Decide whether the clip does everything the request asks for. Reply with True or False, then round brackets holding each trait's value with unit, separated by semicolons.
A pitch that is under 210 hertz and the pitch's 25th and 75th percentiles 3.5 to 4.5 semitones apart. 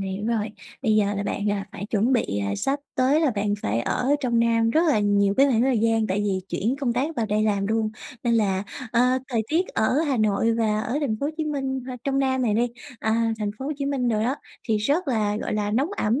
False (225 Hz; 4.0 semitones)